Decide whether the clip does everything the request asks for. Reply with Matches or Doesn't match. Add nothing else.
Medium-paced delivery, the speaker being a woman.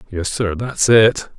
Doesn't match